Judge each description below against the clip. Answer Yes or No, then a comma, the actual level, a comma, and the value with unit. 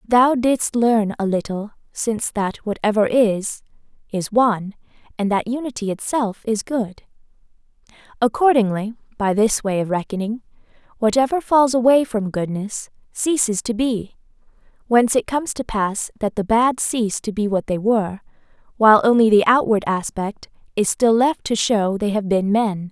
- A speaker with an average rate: Yes, average, 155 wpm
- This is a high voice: Yes, high, 220 Hz